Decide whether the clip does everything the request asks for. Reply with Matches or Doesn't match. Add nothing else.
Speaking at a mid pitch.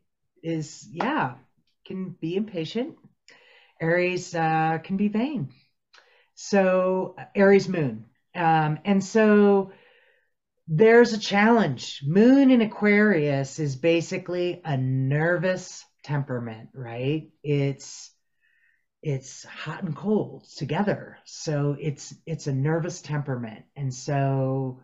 Matches